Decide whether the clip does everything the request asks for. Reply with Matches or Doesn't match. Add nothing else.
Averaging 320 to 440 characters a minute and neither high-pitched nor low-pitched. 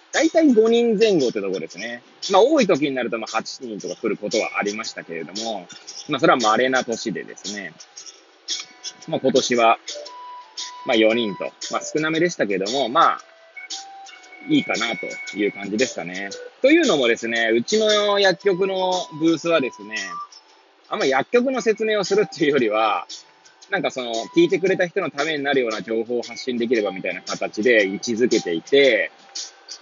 Matches